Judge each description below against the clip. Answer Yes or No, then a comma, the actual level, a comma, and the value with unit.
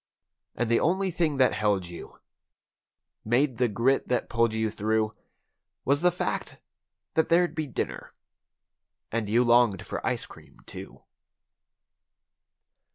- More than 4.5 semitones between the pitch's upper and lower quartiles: Yes, average, 5.2 semitones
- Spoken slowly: Yes, slow, 125 wpm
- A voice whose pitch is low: Yes, low, 120 Hz